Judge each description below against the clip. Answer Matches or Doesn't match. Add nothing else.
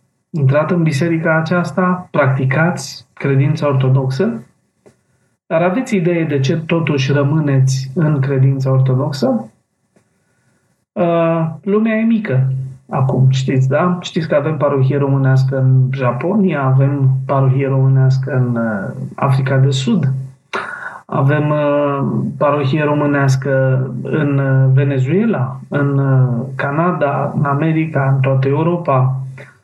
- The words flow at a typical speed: Doesn't match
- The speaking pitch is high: Doesn't match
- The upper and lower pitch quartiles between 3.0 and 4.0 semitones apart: Matches